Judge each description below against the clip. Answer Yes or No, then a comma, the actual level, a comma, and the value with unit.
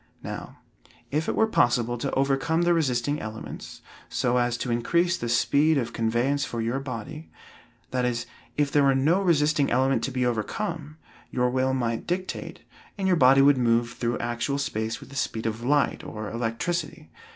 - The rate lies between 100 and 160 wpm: No, average, 175 wpm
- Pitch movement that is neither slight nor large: Yes, average, 3.8 semitones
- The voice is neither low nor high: No, low, 130 Hz